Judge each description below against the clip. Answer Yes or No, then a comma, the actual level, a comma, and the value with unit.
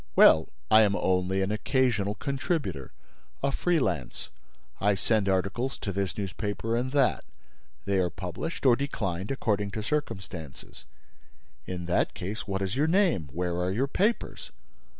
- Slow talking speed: No, average, 150 wpm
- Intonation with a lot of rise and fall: Yes, wide, 6.0 semitones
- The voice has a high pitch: No, low, 100 Hz